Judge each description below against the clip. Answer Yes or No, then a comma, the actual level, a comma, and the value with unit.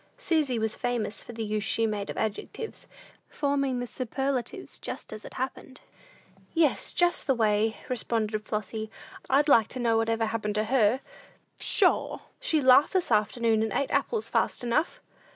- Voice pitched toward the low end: No, high, 235 Hz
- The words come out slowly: No, average, 165 wpm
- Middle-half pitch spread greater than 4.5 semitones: No, average, 3.8 semitones